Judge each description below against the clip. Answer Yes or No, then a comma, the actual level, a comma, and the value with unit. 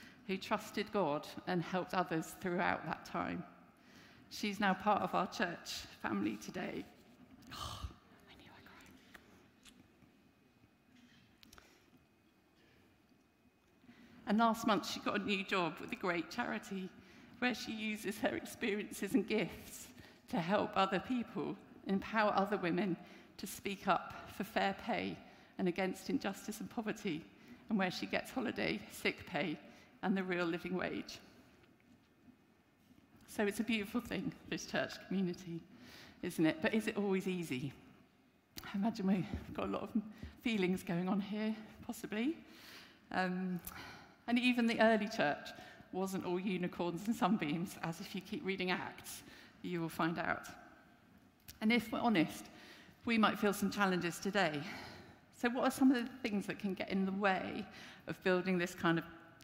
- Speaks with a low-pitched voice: No, high, 195 Hz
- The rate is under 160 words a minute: Yes, average, 150 wpm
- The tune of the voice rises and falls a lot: No, average, 3.7 semitones